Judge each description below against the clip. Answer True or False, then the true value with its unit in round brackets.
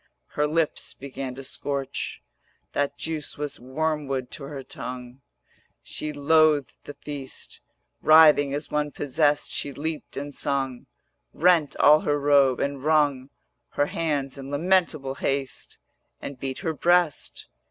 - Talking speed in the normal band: False (130 wpm)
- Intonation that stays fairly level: True (2.1 semitones)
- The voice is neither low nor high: True (145 Hz)